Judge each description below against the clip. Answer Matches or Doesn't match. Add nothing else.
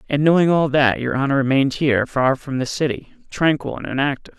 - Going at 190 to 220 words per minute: Matches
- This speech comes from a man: Matches